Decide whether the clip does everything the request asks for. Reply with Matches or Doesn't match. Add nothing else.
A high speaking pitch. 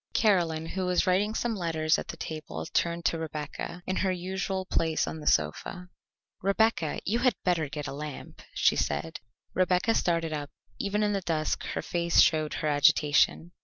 Doesn't match